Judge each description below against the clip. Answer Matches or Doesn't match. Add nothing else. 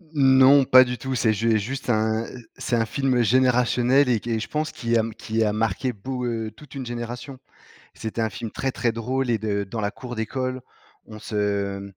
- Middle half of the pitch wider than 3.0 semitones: Doesn't match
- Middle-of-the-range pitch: Doesn't match